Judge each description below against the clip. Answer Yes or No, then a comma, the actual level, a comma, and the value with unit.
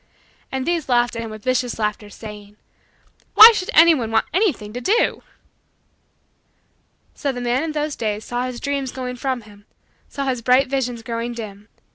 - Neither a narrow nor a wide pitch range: Yes, average, 3.5 semitones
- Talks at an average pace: Yes, average, 170 wpm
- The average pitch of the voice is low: No, high, 245 Hz